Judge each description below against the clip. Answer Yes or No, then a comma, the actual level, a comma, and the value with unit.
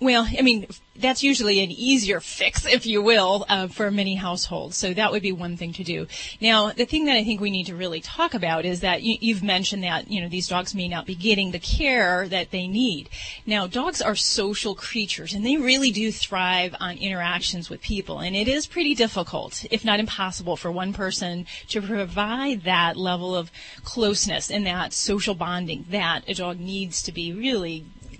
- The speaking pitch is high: Yes, high, 200 Hz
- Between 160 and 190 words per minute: No, fast, 205 wpm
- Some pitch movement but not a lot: Yes, average, 3.6 semitones